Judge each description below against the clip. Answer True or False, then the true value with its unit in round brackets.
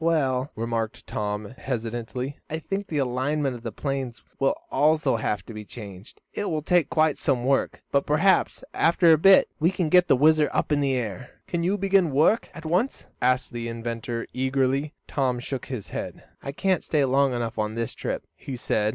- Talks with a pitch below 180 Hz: True (135 Hz)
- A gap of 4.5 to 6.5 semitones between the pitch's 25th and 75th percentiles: True (4.9 semitones)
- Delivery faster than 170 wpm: True (195 wpm)